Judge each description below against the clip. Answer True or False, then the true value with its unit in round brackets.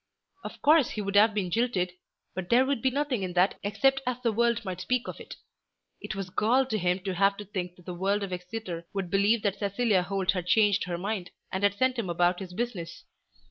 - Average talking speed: False (230 wpm)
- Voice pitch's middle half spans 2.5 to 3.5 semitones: False (4.1 semitones)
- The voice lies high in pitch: True (200 Hz)